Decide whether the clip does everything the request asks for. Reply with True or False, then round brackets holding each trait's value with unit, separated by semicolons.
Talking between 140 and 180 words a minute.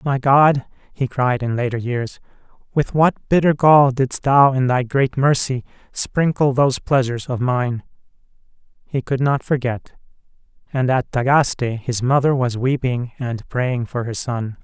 True (155 wpm)